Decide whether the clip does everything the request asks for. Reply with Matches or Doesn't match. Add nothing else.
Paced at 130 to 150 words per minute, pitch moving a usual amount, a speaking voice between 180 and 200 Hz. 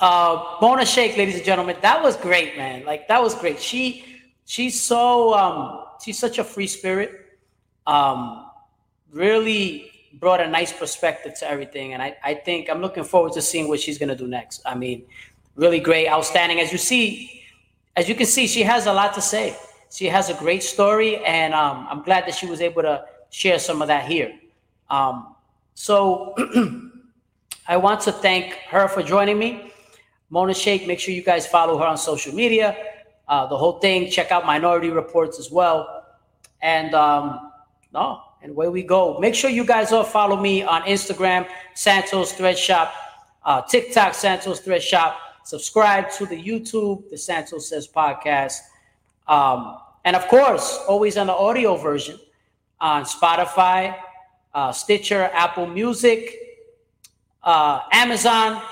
Doesn't match